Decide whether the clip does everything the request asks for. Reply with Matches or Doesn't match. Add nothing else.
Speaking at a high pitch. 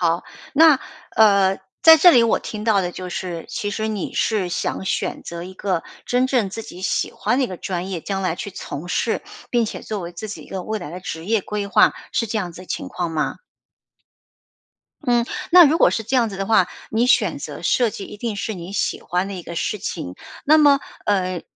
Matches